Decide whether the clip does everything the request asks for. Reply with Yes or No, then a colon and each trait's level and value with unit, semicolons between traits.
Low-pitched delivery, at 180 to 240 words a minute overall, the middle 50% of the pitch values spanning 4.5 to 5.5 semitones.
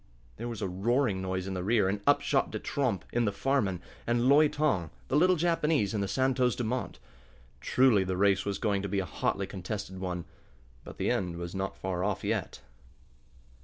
Yes: low, 100 Hz; average, 195 wpm; average, 5.0 semitones